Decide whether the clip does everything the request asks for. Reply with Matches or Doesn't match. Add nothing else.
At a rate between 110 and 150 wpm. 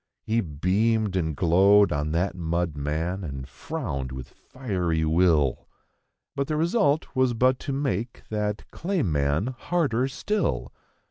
Matches